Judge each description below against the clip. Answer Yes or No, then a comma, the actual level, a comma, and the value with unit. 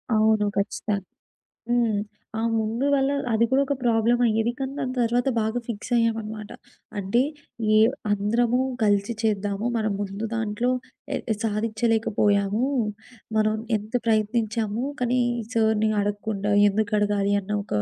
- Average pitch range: No, narrow, 2.1 semitones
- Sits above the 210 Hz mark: Yes, high, 220 Hz